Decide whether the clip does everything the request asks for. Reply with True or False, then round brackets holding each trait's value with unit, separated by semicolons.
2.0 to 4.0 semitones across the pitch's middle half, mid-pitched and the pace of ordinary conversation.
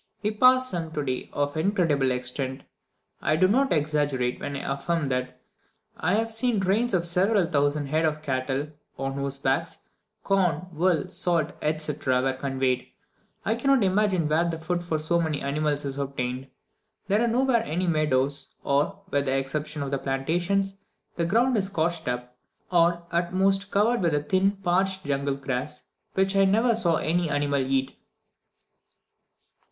False (5.4 semitones; 160 Hz; 160 wpm)